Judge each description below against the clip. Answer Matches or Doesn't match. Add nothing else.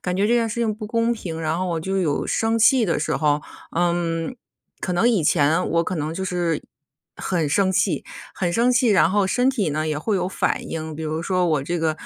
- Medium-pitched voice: Matches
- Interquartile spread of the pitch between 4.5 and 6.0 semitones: Matches